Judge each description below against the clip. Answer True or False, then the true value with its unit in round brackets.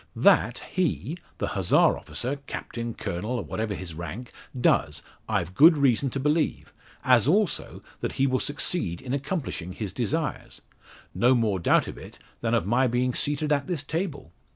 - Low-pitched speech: True (125 Hz)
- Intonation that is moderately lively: True (4.8 semitones)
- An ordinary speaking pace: True (165 wpm)